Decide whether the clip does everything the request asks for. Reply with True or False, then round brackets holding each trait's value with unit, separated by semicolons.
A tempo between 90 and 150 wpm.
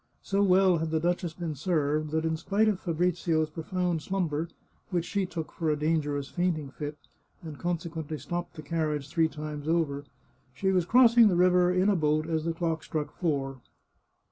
False (180 wpm)